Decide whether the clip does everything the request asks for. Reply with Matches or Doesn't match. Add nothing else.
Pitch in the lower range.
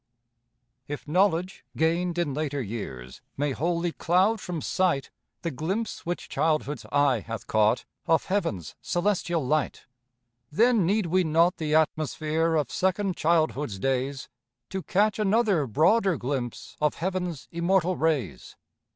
Doesn't match